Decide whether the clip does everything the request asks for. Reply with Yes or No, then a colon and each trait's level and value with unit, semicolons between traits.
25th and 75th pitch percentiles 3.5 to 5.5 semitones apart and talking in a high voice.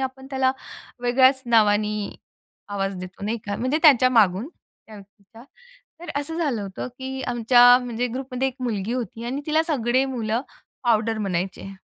Yes: average, 3.8 semitones; high, 240 Hz